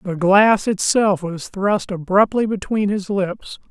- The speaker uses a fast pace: No, average, 145 wpm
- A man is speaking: Yes, male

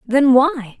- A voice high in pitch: Yes, very high, 260 Hz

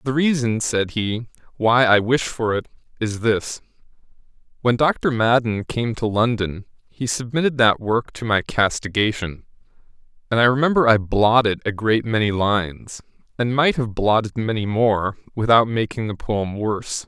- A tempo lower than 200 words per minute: Yes, average, 155 wpm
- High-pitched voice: No, low, 115 Hz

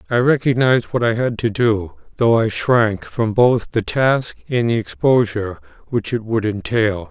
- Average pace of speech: Yes, average, 175 wpm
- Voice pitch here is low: Yes, low, 115 Hz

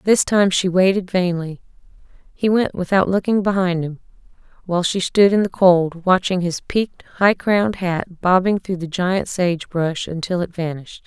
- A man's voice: No, female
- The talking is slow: No, average, 170 wpm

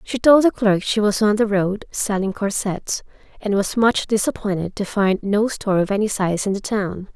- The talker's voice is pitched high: Yes, high, 205 Hz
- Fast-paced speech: Yes, fast, 210 wpm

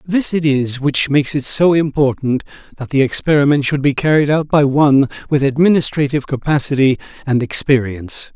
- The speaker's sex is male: Yes, male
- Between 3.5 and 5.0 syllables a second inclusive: No, 5.6 syllables/s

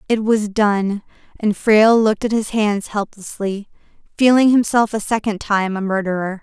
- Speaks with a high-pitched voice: Yes, high, 210 Hz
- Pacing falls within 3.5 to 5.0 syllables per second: Yes, 4.8 syllables/s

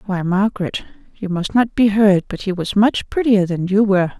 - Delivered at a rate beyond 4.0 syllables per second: Yes, 5.1 syllables/s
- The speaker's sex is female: Yes, female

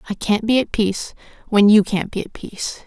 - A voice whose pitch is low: No, high, 210 Hz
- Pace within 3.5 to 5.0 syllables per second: No, 5.7 syllables/s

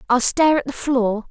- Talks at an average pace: No, fast, 230 wpm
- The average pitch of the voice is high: Yes, very high, 260 Hz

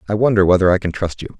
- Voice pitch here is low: Yes, low, 100 Hz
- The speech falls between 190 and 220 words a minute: No, fast, 300 wpm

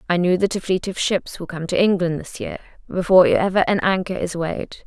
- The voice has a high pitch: No, medium, 180 Hz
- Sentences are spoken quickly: Yes, fast, 235 wpm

